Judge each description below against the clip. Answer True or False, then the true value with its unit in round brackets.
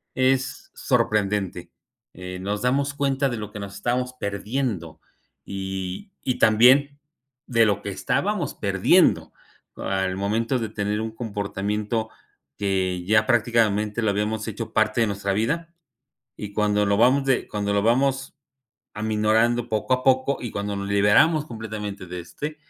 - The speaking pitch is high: False (110 Hz)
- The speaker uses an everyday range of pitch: True (3.6 semitones)